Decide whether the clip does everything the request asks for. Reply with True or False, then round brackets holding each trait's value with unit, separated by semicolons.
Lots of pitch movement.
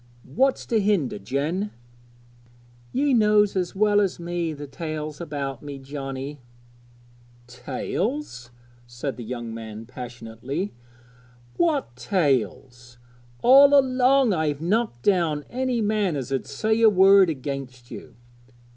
True (8.1 semitones)